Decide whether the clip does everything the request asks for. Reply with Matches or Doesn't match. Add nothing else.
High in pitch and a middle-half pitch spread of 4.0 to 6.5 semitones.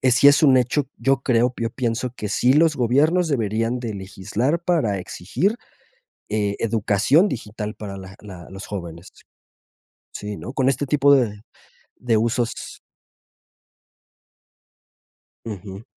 Doesn't match